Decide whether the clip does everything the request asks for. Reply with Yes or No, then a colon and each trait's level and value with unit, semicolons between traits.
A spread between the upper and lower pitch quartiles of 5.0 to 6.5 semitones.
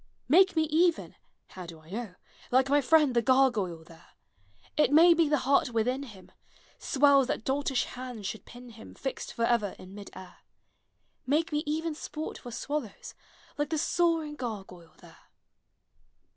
Yes: wide, 5.5 semitones